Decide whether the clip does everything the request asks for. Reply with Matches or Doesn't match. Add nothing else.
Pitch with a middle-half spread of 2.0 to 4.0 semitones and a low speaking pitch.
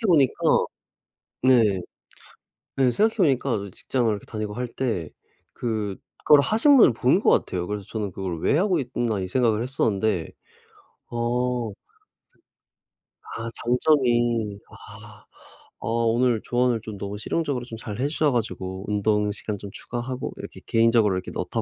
Matches